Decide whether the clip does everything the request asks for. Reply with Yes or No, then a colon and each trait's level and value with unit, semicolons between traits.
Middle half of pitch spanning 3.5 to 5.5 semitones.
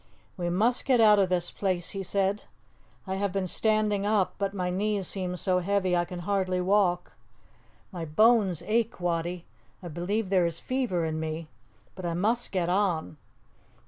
No: average, 2.8 semitones